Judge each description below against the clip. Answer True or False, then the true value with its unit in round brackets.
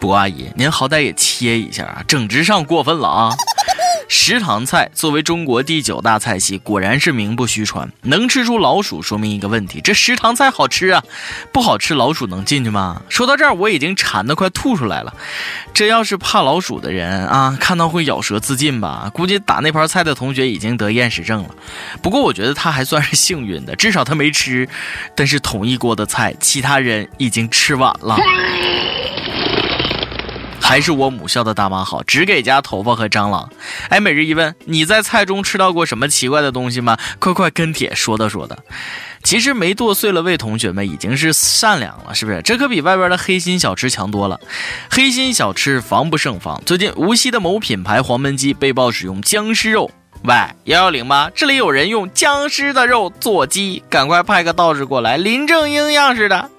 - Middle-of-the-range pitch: True (145 Hz)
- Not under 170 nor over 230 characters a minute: False (295 characters per minute)